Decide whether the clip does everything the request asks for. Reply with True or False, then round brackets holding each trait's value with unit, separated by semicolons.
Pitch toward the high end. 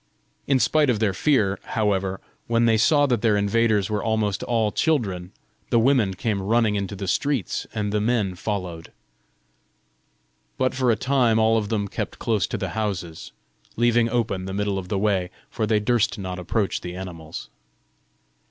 False (105 Hz)